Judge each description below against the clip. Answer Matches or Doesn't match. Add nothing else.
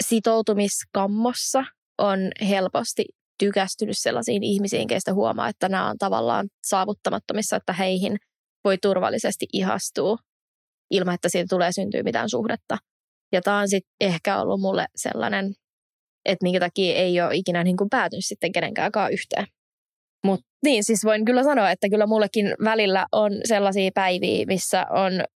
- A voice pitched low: Doesn't match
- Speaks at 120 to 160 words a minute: Matches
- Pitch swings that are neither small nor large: Doesn't match